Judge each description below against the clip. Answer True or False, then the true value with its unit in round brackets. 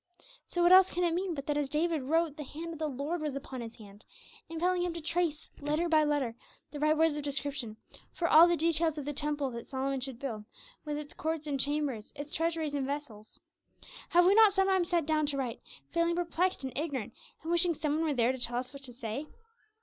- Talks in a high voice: True (300 Hz)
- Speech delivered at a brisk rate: True (230 wpm)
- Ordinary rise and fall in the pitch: True (3.6 semitones)